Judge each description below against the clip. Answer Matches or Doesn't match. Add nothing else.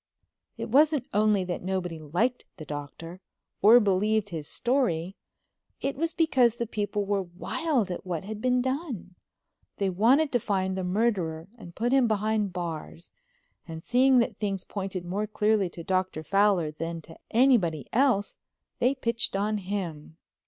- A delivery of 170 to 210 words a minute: Doesn't match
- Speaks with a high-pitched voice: Matches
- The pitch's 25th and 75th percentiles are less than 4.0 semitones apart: Doesn't match